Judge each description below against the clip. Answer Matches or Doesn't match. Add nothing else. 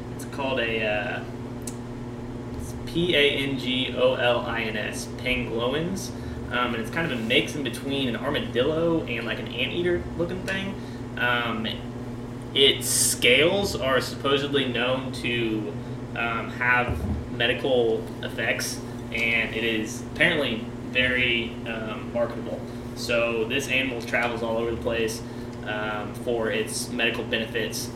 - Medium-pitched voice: Doesn't match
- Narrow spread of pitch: Matches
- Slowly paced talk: Matches